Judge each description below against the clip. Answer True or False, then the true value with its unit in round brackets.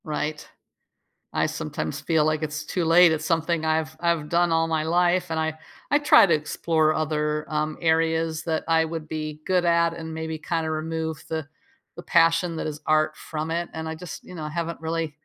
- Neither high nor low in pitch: True (160 Hz)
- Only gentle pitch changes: True (1.2 semitones)